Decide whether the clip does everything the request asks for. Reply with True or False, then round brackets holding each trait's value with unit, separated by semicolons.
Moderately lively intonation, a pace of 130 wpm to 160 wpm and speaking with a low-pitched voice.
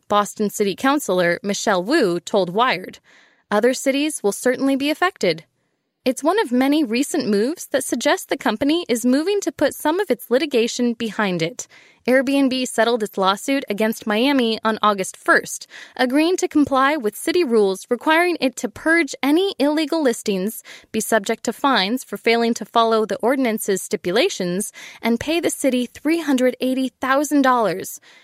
False (4.6 semitones; 155 wpm; 250 Hz)